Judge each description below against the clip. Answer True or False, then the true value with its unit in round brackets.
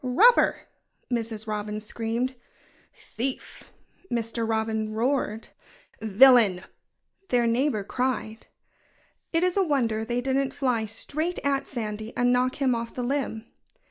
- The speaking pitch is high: True (240 Hz)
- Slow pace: True (120 wpm)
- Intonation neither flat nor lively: True (3.2 semitones)